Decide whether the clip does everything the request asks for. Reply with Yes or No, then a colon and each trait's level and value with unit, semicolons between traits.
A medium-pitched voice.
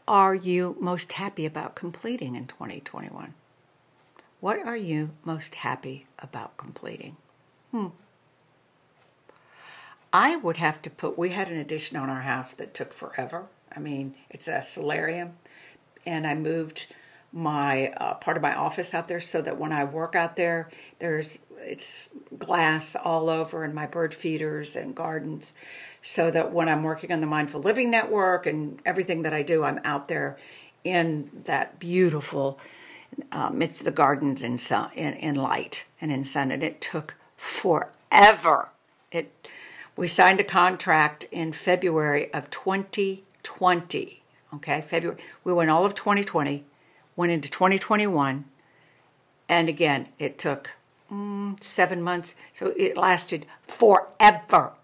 Yes: medium, 165 Hz